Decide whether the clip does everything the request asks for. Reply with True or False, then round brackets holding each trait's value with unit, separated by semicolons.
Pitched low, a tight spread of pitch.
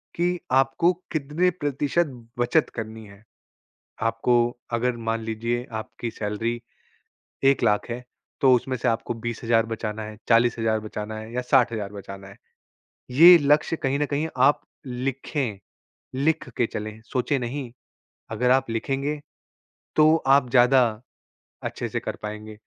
False (120 Hz; 3.7 semitones)